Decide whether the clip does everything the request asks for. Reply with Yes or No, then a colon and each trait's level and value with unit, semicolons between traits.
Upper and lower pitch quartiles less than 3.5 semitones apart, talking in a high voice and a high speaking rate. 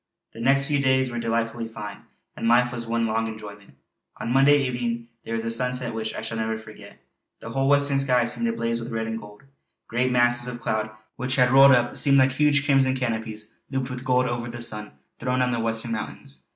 No: narrow, 2.4 semitones; low, 120 Hz; fast, 215 wpm